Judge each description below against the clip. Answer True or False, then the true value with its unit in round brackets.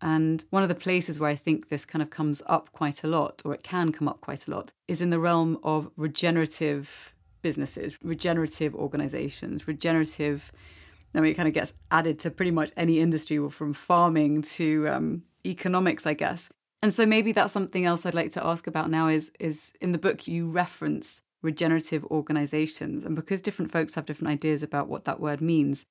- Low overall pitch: False (160 Hz)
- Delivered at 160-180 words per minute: False (200 wpm)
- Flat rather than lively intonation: True (1.9 semitones)